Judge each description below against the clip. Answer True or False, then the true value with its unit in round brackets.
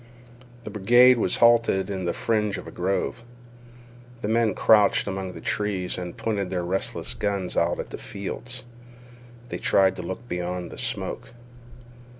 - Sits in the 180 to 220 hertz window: False (100 Hz)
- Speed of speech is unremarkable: True (155 wpm)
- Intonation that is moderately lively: True (3.4 semitones)